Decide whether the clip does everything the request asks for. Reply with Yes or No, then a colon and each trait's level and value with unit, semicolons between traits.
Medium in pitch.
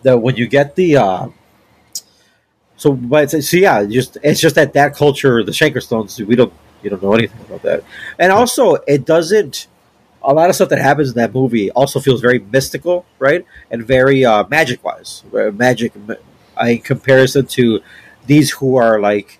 No: low, 130 Hz